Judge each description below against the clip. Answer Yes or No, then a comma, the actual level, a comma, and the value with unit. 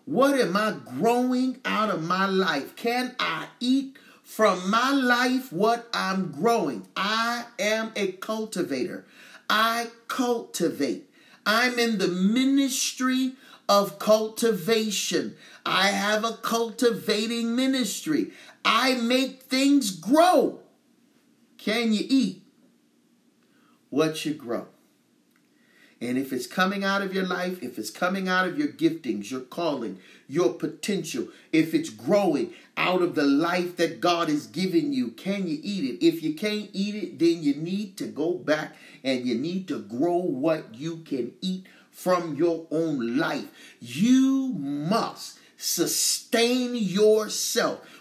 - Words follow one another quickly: No, slow, 135 wpm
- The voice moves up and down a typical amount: No, wide, 6.1 semitones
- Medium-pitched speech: No, high, 215 Hz